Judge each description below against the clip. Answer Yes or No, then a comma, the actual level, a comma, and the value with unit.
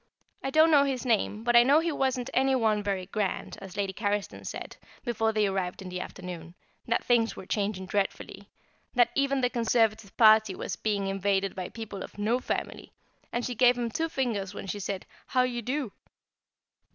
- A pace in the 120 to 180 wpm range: No, average, 190 wpm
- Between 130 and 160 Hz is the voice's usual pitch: No, high, 220 Hz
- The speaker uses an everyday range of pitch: Yes, average, 4.0 semitones